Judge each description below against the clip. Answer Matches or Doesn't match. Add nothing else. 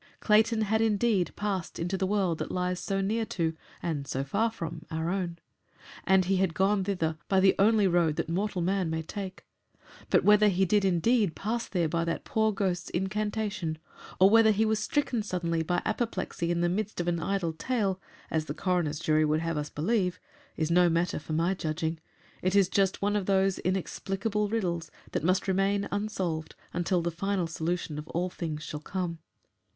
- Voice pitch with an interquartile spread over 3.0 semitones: Matches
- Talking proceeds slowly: Doesn't match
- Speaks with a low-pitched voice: Doesn't match